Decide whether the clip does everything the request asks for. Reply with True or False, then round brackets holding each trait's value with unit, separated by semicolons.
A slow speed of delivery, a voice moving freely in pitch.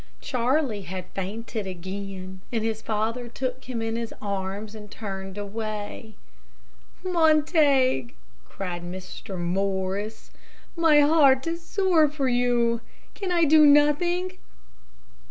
True (115 wpm; 7.0 semitones)